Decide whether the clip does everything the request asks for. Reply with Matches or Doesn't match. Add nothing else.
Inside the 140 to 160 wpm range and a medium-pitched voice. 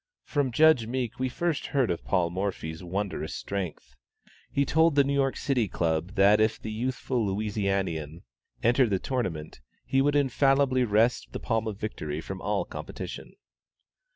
Doesn't match